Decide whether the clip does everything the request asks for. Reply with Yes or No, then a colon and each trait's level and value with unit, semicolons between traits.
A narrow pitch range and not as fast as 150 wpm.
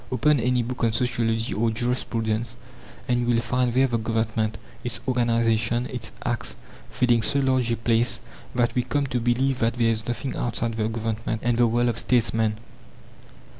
No: narrow, 1.5 semitones; average, 175 wpm